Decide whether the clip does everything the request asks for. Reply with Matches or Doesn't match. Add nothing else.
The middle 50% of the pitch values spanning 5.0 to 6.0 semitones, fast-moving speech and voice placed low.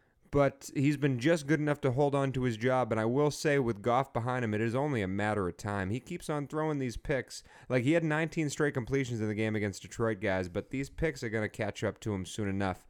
Matches